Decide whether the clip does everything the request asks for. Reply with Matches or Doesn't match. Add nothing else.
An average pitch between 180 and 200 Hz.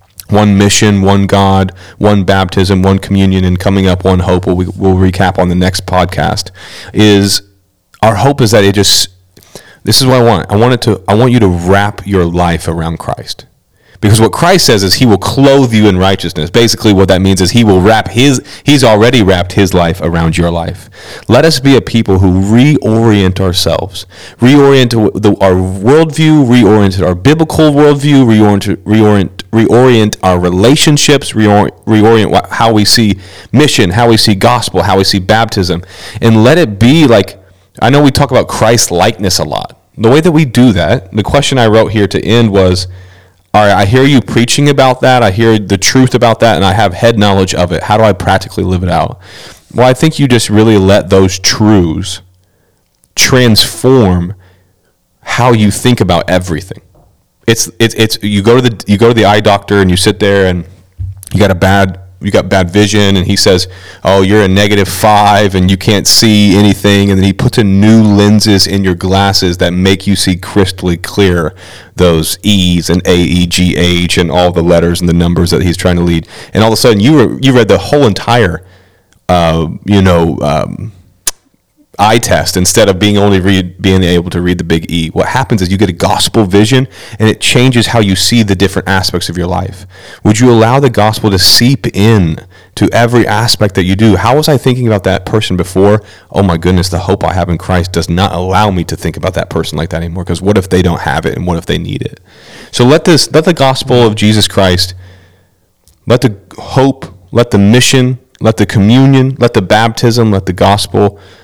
Doesn't match